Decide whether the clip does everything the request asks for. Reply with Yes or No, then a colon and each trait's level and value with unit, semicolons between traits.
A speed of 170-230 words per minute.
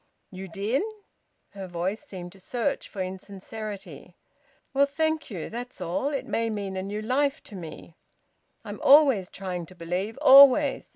No: average, 155 wpm